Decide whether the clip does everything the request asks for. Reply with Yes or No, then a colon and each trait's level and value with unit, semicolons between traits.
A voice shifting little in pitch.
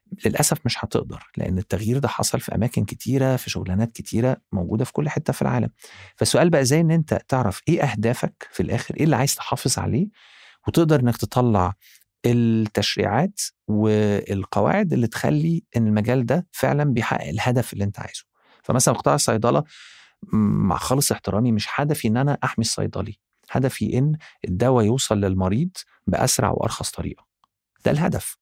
No: average, 4.9 semitones